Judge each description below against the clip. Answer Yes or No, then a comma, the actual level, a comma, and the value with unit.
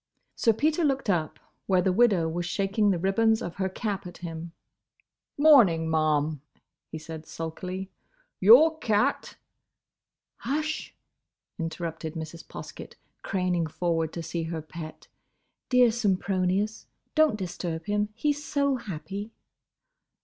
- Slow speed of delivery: Yes, slow, 120 wpm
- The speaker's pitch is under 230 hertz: Yes, high, 190 Hz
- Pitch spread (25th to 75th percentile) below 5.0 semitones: No, wide, 5.6 semitones